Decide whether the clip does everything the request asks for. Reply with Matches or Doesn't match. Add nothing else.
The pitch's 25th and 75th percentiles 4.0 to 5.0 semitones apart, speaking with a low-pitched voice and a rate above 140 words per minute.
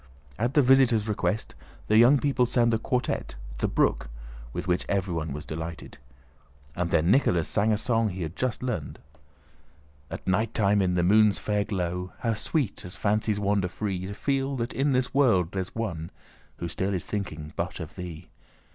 Matches